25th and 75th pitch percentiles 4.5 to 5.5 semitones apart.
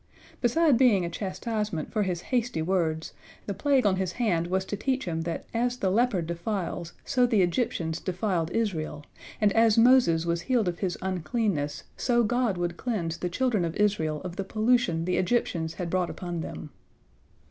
Yes: average, 5.2 semitones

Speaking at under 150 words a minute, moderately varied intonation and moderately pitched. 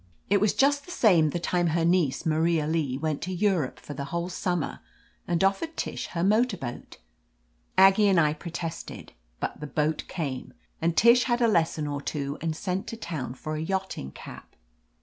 No: average, 190 wpm; average, 4.0 semitones; medium, 170 Hz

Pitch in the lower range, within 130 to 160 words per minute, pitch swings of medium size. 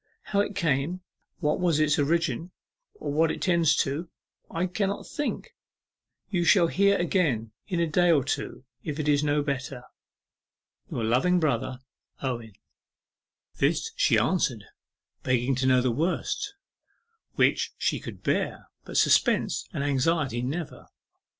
No: medium, 155 Hz; average, 140 wpm; average, 4.8 semitones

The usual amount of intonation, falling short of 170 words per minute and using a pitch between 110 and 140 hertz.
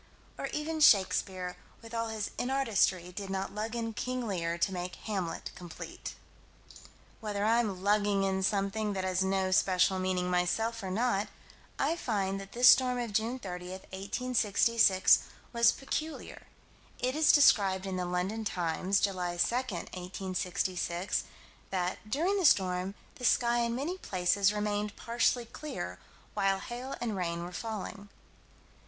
No: average, 4.0 semitones; average, 145 wpm; high, 200 Hz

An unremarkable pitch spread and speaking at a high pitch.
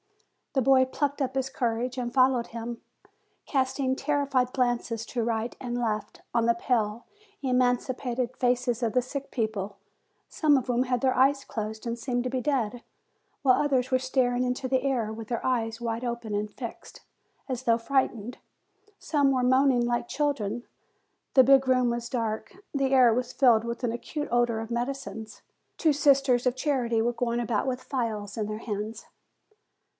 No: narrow, 2.1 semitones; high, 245 Hz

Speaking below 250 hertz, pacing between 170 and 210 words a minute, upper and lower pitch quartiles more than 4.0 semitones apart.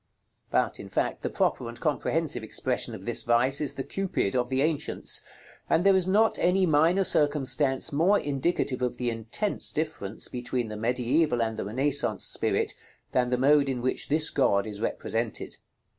Yes: low, 135 Hz; average, 175 wpm; average, 4.5 semitones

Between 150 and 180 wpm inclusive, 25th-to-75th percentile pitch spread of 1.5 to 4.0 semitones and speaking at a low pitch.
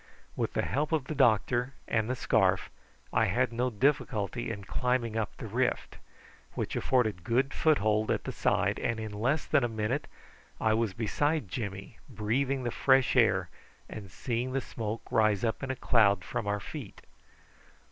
Yes: average, 170 wpm; average, 3.4 semitones; low, 115 Hz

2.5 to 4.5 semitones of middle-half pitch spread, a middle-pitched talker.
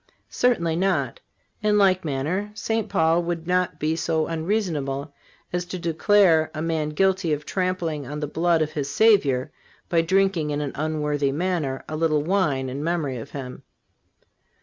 Yes: average, 3.7 semitones; medium, 160 Hz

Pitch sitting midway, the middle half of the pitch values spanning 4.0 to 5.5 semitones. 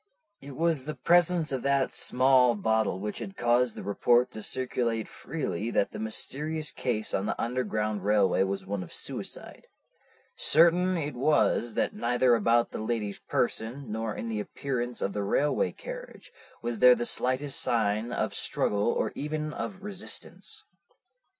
No: low, 120 Hz; average, 5.2 semitones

